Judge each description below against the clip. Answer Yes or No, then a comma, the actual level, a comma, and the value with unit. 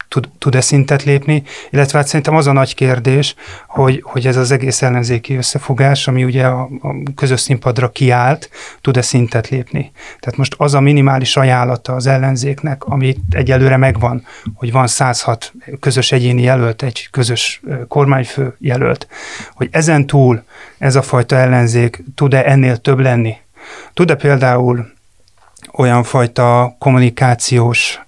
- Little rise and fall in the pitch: Yes, narrow, 2.0 semitones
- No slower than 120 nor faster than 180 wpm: Yes, average, 135 wpm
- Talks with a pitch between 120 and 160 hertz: Yes, low, 130 Hz